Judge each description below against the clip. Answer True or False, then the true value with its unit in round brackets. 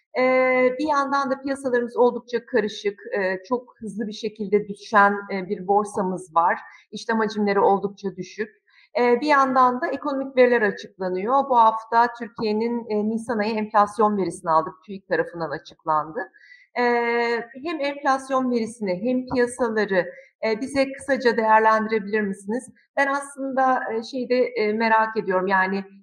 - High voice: True (225 Hz)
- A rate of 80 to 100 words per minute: False (135 wpm)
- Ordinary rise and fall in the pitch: True (3.8 semitones)